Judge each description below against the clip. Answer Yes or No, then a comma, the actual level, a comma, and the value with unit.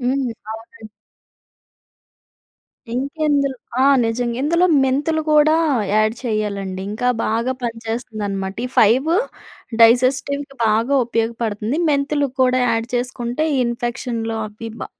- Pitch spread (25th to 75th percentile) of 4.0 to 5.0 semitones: No, average, 3.5 semitones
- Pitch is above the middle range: Yes, high, 240 Hz